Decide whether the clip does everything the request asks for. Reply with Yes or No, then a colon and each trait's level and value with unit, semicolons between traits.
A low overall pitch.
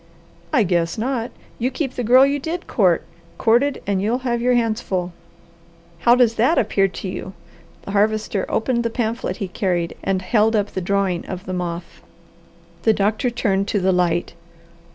No: high, 215 Hz